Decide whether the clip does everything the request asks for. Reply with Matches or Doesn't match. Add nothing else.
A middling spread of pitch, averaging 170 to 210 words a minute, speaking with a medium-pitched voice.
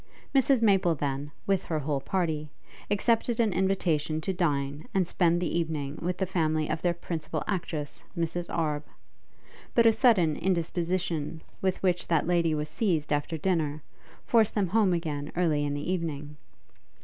Doesn't match